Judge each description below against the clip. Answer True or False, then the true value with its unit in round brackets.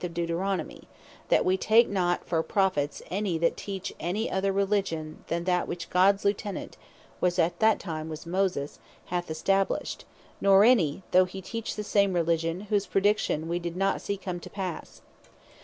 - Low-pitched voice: False (185 Hz)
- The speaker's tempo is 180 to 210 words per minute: False (170 wpm)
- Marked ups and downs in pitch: False (2.7 semitones)